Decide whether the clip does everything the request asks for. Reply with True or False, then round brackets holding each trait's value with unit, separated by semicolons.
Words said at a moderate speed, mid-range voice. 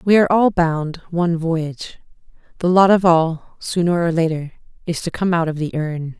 True (195 wpm; 170 Hz)